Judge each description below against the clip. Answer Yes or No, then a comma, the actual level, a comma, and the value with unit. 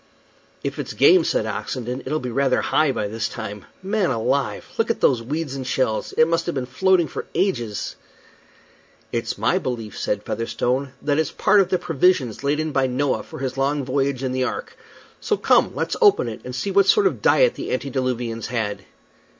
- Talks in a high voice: No, low, 135 Hz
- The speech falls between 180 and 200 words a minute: Yes, average, 195 wpm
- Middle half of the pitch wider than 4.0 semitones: Yes, average, 5.1 semitones